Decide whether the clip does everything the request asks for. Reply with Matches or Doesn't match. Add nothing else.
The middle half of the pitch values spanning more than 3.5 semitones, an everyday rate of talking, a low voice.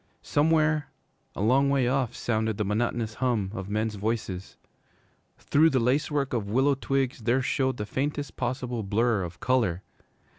Matches